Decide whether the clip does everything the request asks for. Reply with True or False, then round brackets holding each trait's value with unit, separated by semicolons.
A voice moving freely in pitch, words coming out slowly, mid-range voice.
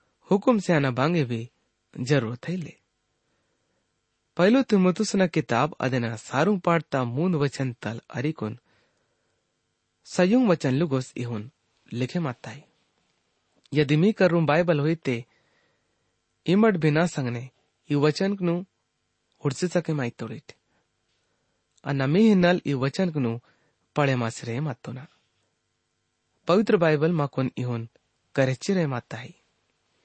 True (6.3 semitones; 115 wpm; 145 Hz)